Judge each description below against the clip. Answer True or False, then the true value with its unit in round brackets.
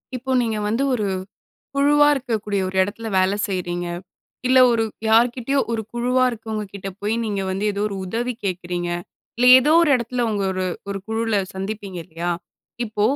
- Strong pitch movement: False (3.7 semitones)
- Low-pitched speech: False (220 Hz)